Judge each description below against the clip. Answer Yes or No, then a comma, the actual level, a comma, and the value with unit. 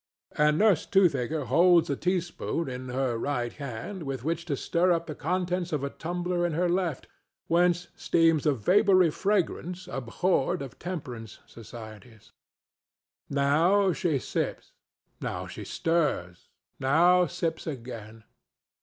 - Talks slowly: Yes, slow, 125 wpm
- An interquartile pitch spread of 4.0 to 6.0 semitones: Yes, average, 5.2 semitones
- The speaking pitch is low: No, medium, 160 Hz